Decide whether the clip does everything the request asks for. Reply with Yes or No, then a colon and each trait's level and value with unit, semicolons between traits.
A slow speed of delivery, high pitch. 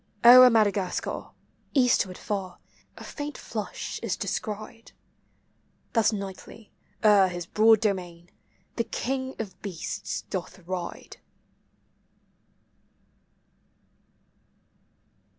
Yes: slow, 85 wpm; high, 210 Hz